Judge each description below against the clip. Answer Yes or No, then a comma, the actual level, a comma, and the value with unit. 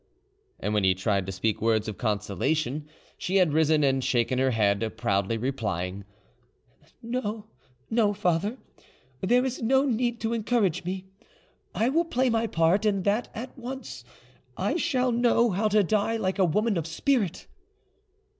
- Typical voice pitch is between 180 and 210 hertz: Yes, high, 190 Hz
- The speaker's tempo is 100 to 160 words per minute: Yes, average, 155 wpm